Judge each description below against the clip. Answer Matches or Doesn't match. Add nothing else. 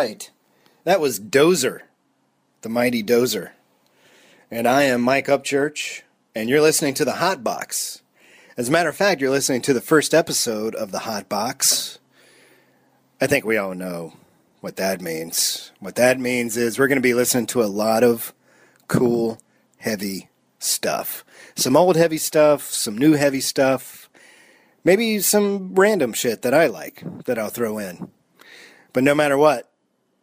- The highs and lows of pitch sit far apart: Doesn't match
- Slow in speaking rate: Doesn't match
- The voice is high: Doesn't match